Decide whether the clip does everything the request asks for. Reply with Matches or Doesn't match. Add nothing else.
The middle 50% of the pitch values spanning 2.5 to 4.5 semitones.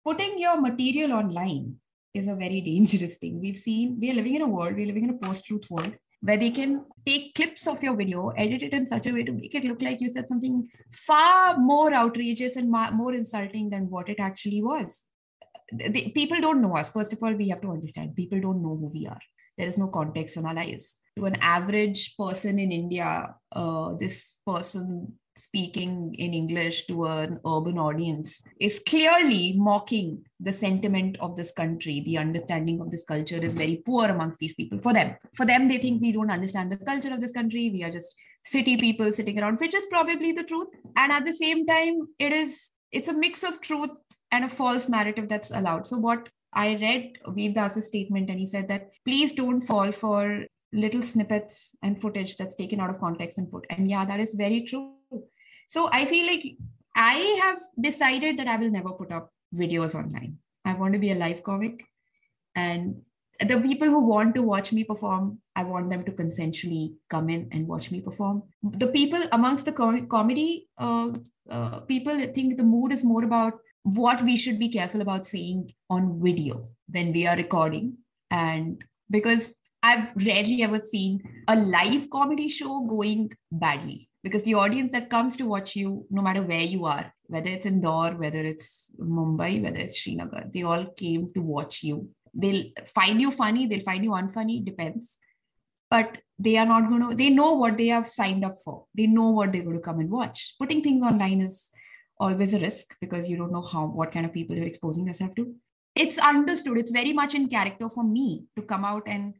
Doesn't match